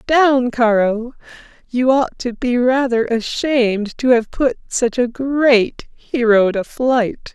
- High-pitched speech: Yes, high, 245 Hz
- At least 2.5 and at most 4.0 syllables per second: Yes, 3.5 syllables/s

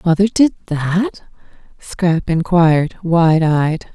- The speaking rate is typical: No, slow, 105 wpm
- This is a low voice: No, medium, 170 Hz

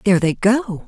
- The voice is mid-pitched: No, high, 200 Hz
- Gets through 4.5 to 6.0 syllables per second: Yes, 5.3 syllables/s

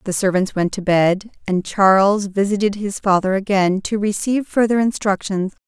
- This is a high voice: Yes, high, 200 Hz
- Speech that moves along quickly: No, average, 160 wpm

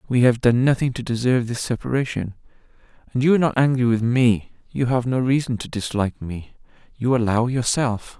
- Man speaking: Yes, male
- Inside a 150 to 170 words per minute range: No, average, 185 wpm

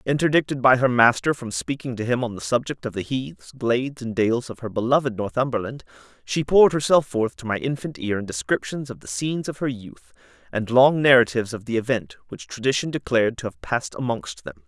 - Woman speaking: No, male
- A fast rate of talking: Yes, fast, 210 wpm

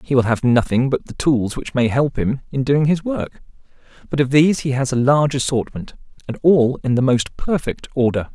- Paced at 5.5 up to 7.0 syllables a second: No, 5.2 syllables/s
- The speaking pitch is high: No, low, 135 Hz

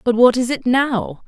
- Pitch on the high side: Yes, high, 240 Hz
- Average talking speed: No, fast, 235 wpm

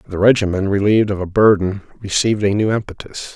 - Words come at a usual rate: Yes, average, 180 wpm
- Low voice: Yes, low, 100 Hz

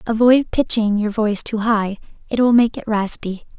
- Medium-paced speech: Yes, average, 165 wpm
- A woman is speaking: Yes, female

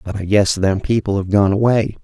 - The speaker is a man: Yes, male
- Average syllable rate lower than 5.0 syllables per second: No, 5.3 syllables/s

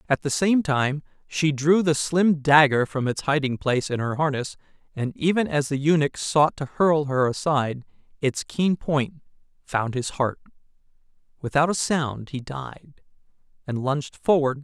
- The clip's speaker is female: No, male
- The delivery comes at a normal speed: Yes, average, 175 wpm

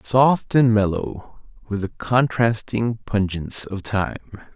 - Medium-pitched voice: No, low, 110 Hz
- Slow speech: Yes, slow, 120 wpm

